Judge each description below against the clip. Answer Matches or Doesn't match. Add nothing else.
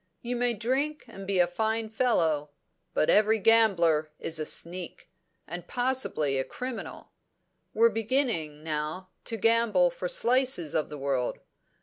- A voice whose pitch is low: Doesn't match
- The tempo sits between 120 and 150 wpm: Matches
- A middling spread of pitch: Doesn't match